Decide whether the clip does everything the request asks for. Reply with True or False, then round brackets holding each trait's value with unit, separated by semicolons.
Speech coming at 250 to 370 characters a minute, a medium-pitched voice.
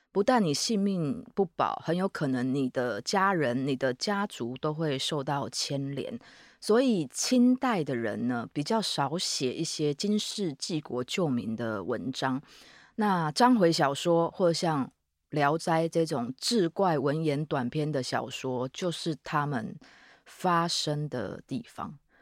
False (210 characters per minute; 155 Hz)